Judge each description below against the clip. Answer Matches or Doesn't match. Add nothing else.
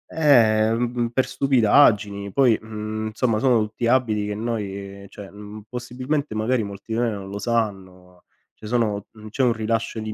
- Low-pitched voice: Matches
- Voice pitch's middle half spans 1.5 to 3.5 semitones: Matches